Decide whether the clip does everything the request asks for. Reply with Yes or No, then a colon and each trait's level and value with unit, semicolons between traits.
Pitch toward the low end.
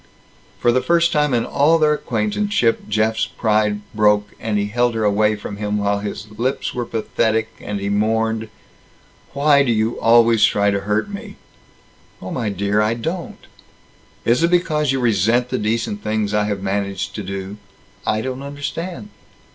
Yes: low, 110 Hz